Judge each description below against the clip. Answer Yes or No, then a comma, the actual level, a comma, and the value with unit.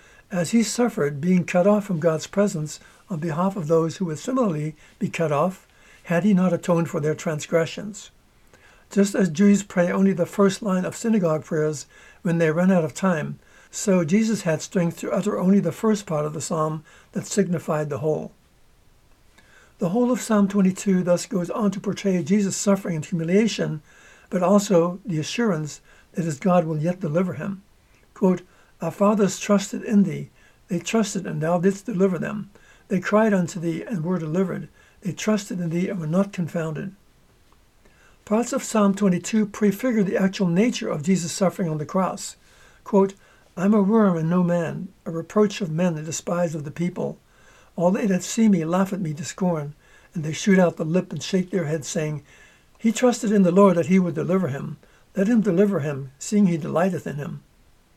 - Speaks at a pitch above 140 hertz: Yes, medium, 185 Hz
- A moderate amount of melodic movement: Yes, average, 3.3 semitones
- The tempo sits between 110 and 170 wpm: No, average, 190 wpm